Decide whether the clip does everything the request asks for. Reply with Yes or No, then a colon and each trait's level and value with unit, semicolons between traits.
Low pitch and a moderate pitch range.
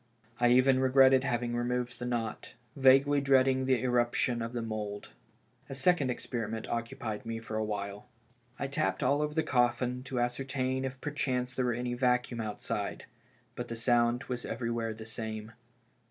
No: low, 125 Hz; narrow, 2.2 semitones